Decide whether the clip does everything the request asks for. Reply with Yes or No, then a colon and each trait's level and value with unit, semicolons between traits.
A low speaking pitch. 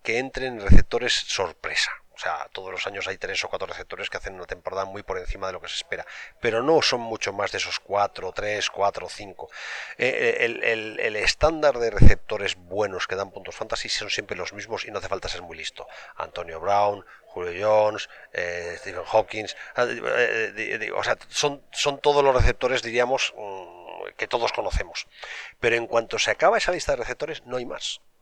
Yes: low, 125 Hz